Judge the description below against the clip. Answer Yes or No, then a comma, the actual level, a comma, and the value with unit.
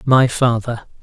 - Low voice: Yes, low, 120 Hz